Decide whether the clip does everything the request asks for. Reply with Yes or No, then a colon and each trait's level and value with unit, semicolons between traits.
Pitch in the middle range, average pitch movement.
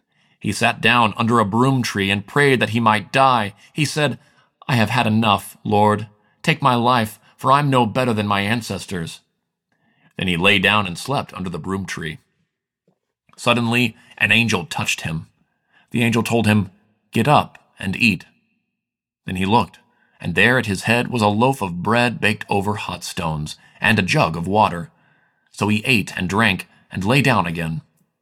No: low, 110 Hz; average, 3.5 semitones